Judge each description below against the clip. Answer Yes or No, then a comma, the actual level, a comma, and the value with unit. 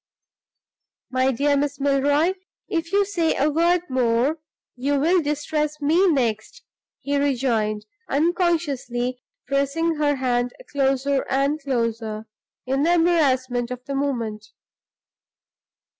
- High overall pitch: Yes, very high, 280 Hz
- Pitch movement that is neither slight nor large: Yes, average, 3.4 semitones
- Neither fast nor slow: No, slow, 115 wpm